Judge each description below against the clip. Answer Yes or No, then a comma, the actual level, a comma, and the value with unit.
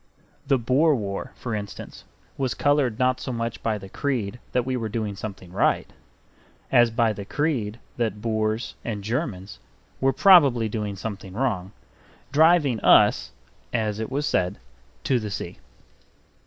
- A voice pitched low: Yes, low, 115 Hz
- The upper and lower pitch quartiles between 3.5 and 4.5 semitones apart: Yes, average, 3.9 semitones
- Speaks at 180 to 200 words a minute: No, average, 150 wpm